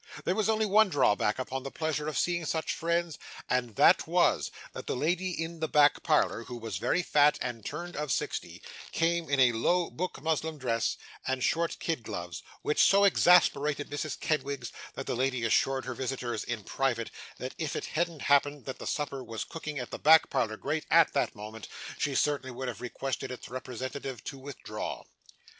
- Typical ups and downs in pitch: Yes, average, 4.4 semitones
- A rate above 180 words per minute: Yes, average, 190 wpm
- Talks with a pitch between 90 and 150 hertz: Yes, medium, 140 Hz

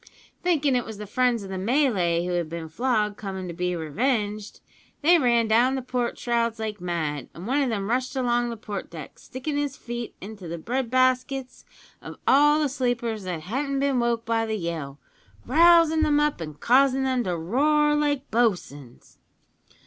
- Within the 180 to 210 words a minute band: Yes, average, 185 wpm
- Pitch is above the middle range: Yes, high, 235 Hz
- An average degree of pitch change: No, wide, 5.8 semitones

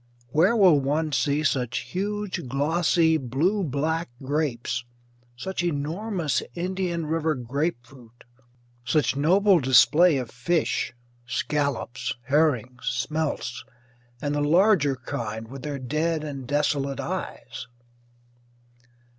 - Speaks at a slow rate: Yes, slow, 105 wpm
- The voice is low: No, medium, 145 Hz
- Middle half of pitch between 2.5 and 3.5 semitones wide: No, average, 4.4 semitones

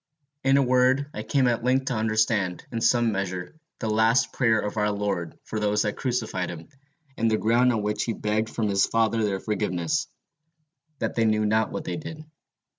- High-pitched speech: No, low, 110 Hz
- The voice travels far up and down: No, average, 3.0 semitones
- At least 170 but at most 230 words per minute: Yes, average, 195 wpm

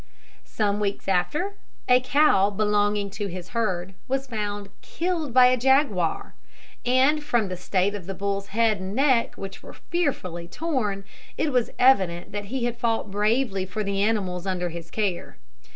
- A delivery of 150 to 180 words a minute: Yes, average, 165 wpm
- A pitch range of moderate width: Yes, average, 4.7 semitones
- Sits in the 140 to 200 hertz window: No, high, 210 Hz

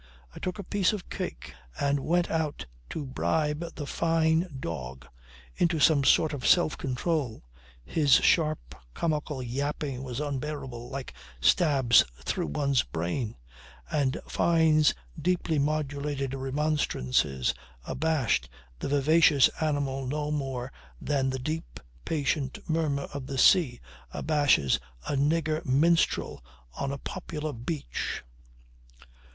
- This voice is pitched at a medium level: Yes, medium, 145 Hz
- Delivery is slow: Yes, slow, 120 wpm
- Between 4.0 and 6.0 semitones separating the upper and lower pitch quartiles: No, average, 3.1 semitones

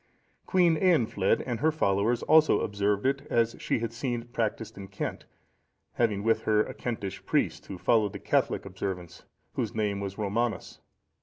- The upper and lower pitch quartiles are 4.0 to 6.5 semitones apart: No, average, 3.3 semitones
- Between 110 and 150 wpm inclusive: No, average, 165 wpm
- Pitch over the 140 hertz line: No, low, 110 Hz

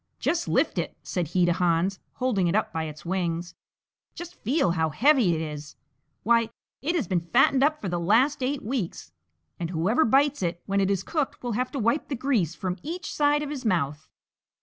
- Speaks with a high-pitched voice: Yes, high, 205 Hz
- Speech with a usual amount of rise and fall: No, wide, 8.0 semitones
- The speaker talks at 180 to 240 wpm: Yes, fast, 205 wpm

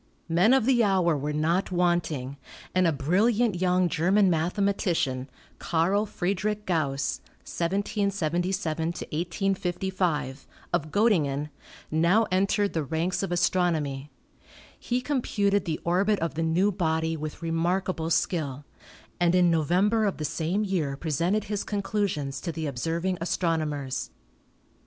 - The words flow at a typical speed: No, slow, 125 wpm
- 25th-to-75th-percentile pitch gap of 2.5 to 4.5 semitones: Yes, average, 3.7 semitones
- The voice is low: No, medium, 175 Hz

